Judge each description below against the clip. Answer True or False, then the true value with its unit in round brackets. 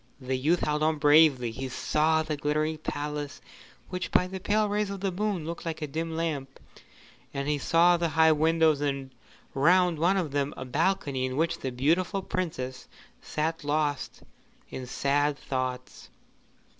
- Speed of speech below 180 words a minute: True (165 wpm)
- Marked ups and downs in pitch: False (3.3 semitones)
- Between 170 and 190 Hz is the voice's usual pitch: False (155 Hz)